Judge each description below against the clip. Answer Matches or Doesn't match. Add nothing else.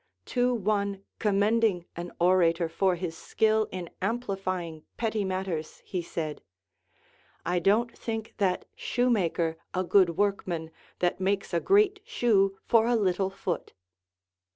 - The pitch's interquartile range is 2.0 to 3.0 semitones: Doesn't match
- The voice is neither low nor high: Doesn't match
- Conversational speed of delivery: Doesn't match